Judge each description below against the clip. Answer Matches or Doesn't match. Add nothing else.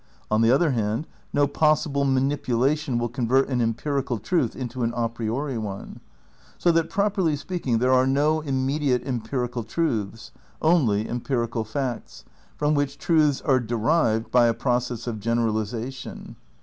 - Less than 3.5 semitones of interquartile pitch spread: Doesn't match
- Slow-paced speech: Doesn't match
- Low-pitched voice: Matches